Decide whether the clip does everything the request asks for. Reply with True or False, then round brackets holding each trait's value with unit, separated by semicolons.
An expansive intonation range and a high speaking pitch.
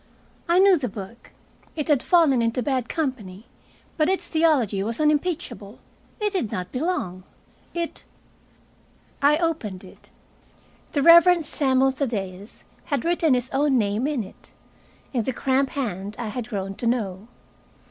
True (6.5 semitones; 260 Hz)